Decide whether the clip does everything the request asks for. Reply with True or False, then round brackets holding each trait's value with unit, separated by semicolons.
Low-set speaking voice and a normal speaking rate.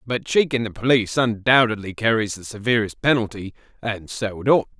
True (115 Hz; 165 wpm)